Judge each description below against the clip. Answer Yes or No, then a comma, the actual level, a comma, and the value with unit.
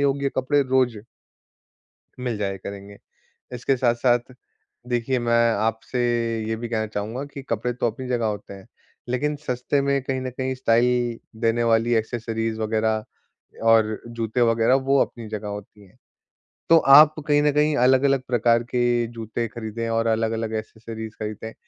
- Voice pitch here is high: No, low, 115 Hz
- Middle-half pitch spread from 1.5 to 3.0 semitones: Yes, narrow, 2.4 semitones